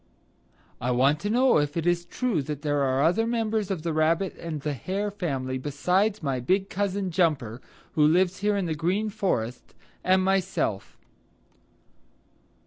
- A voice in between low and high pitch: Yes, medium, 170 Hz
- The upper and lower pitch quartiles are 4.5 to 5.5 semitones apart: Yes, average, 5.2 semitones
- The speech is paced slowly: No, average, 165 wpm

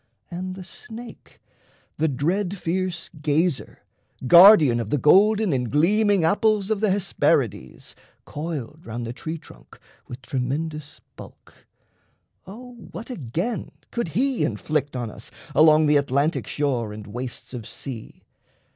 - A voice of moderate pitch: Yes, medium, 155 Hz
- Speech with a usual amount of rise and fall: No, wide, 6.8 semitones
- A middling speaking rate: No, slow, 130 wpm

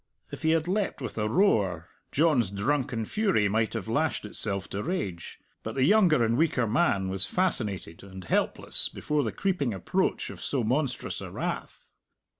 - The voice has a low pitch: Yes, low, 120 Hz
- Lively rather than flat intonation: Yes, wide, 8.0 semitones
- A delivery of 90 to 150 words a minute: No, average, 170 wpm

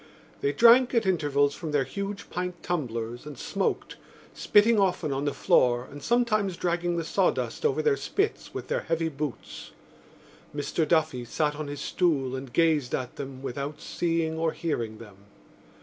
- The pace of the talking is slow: No, average, 165 wpm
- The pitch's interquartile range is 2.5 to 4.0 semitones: No, average, 4.8 semitones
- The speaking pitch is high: No, medium, 155 Hz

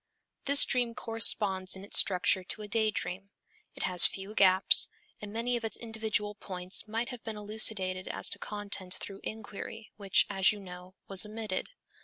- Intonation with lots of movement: No, average, 2.7 semitones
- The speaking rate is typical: Yes, average, 175 wpm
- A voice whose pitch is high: Yes, high, 205 Hz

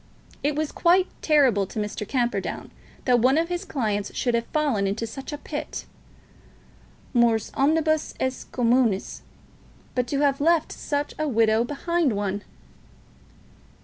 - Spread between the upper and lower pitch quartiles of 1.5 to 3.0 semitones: No, average, 5.1 semitones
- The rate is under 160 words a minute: Yes, average, 140 wpm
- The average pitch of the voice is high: Yes, very high, 260 Hz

